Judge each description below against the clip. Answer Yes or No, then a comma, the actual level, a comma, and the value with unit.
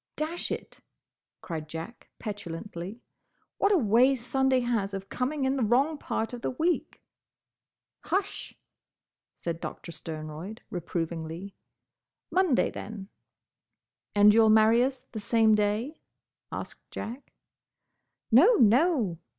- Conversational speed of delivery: No, slow, 115 wpm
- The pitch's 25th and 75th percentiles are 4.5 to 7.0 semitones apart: Yes, average, 5.3 semitones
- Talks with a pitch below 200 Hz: No, high, 225 Hz